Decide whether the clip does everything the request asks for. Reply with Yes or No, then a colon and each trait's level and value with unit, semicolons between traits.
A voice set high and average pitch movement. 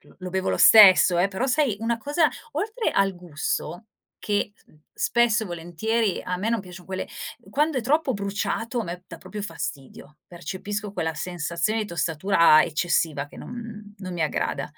Yes: high, 195 Hz; average, 4.6 semitones